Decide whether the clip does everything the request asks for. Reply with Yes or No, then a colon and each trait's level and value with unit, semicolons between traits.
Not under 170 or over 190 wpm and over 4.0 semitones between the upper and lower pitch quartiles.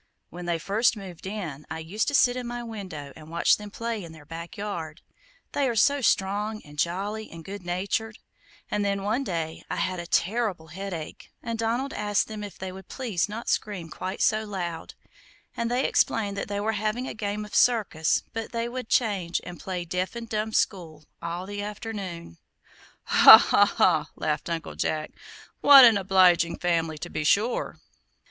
Yes: average, 185 wpm; average, 4.4 semitones